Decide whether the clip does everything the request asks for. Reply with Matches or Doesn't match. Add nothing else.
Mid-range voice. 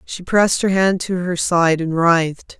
Matches